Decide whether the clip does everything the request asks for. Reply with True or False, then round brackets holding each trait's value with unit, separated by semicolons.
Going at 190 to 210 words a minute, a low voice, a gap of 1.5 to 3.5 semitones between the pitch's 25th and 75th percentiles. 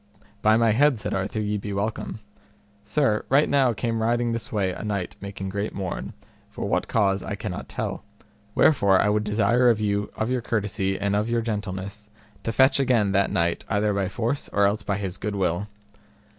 True (195 wpm; 105 Hz; 2.6 semitones)